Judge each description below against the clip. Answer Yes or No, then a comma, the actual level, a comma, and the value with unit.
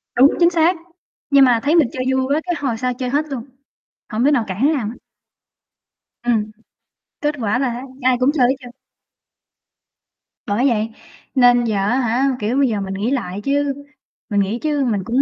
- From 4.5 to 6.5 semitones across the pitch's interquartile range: No, average, 3.9 semitones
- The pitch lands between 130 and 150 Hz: No, very high, 250 Hz